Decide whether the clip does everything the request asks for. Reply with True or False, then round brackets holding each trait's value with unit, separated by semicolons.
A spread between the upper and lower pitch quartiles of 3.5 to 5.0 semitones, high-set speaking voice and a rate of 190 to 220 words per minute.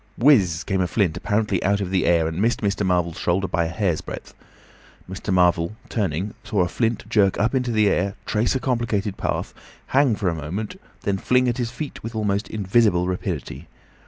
False (4.0 semitones; 100 Hz; 200 wpm)